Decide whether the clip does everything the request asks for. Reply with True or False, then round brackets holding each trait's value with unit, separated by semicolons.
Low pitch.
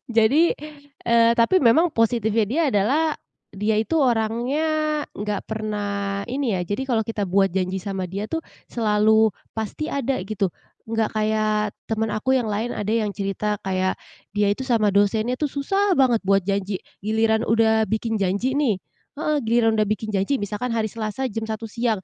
False (220 Hz)